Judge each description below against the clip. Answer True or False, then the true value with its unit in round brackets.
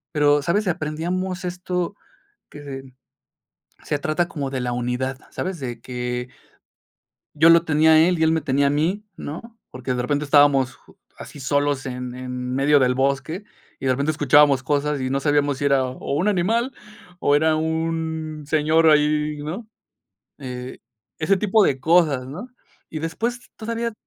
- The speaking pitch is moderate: True (150 Hz)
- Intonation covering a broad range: False (3.6 semitones)